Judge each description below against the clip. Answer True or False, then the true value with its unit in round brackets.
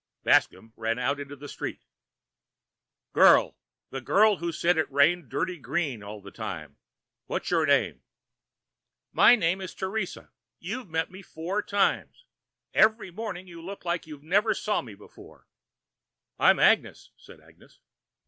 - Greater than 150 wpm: False (145 wpm)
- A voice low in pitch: False (170 Hz)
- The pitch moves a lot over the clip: True (6.0 semitones)